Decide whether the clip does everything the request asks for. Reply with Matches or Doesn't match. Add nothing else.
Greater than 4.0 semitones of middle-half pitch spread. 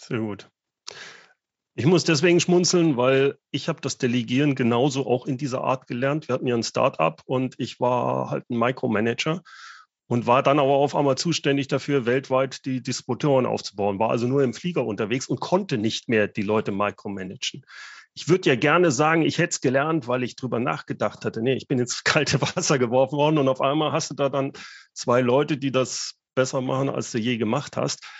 Doesn't match